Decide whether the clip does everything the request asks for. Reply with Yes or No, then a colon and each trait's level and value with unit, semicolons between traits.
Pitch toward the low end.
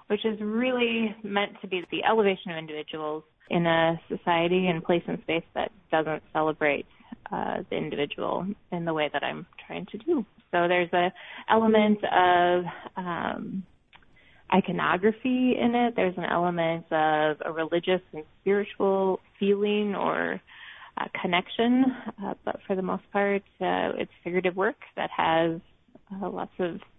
No: medium, 185 Hz